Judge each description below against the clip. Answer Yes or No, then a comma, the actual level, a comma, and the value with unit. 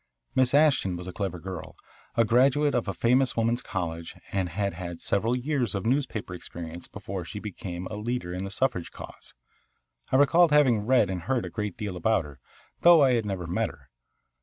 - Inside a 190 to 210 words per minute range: Yes, average, 195 wpm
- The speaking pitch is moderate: No, low, 105 Hz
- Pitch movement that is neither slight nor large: No, wide, 5.8 semitones